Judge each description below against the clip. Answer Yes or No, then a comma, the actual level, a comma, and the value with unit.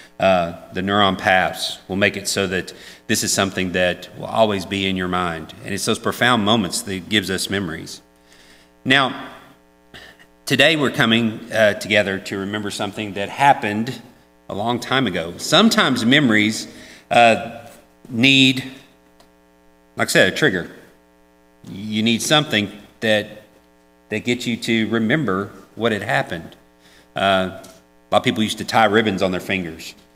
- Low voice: Yes, low, 100 Hz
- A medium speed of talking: Yes, average, 150 wpm